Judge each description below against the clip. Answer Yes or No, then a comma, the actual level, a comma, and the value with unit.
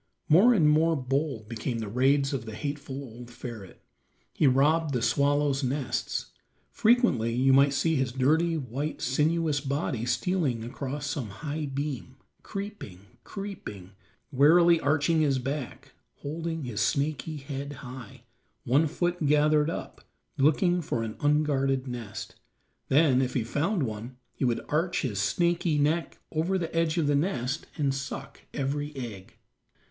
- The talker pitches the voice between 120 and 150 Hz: Yes, medium, 140 Hz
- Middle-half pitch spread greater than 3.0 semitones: Yes, average, 3.7 semitones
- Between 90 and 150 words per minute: Yes, average, 145 wpm